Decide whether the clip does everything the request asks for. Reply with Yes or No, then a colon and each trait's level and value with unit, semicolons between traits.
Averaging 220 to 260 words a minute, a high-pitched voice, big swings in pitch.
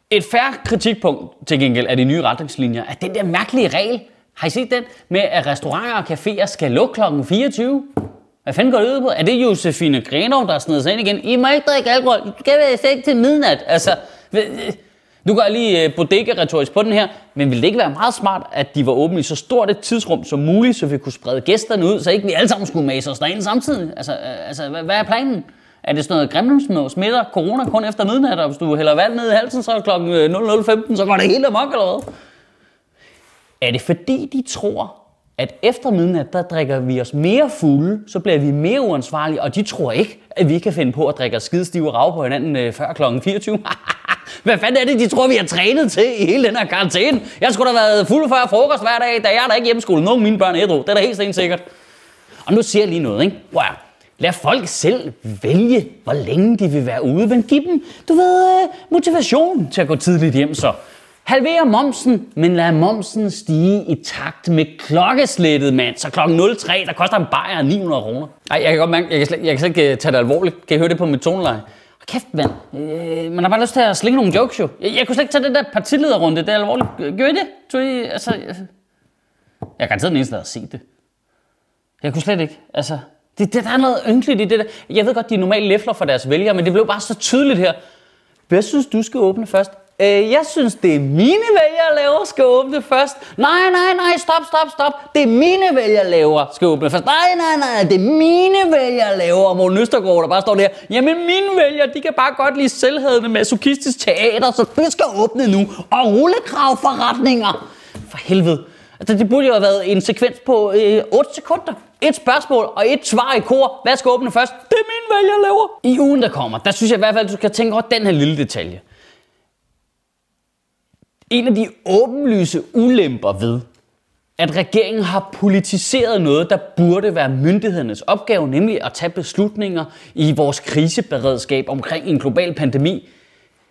Yes: fast, 225 wpm; high, 210 Hz; wide, 7.3 semitones